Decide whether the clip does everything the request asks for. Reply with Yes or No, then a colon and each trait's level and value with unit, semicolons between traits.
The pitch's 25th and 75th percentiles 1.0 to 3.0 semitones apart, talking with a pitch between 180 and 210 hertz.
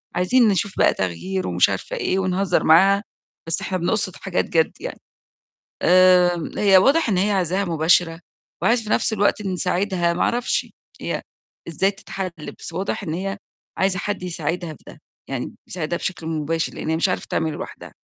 Yes: average, 2.7 semitones; medium, 185 Hz